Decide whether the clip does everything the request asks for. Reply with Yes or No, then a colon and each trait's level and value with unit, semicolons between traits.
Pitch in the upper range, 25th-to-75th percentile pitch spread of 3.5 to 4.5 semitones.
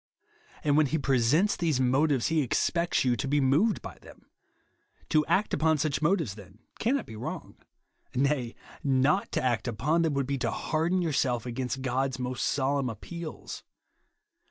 No: medium, 140 Hz; average, 3.8 semitones